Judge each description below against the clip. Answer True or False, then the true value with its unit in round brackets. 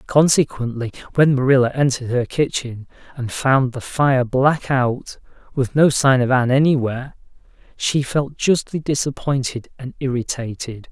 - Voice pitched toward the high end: False (130 Hz)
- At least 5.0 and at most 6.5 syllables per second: False (4.7 syllables/s)